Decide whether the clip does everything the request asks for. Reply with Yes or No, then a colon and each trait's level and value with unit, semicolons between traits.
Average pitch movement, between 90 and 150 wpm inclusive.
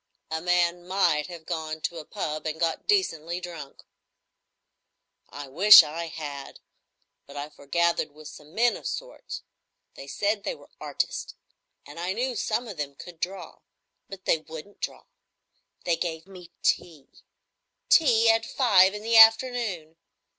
Yes: average, 5.0 semitones; average, 145 wpm